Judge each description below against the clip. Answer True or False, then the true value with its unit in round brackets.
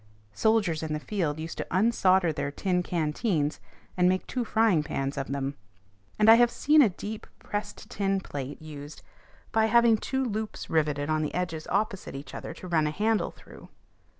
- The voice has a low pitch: False (180 Hz)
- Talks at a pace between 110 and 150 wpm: False (180 wpm)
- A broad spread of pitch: True (6.1 semitones)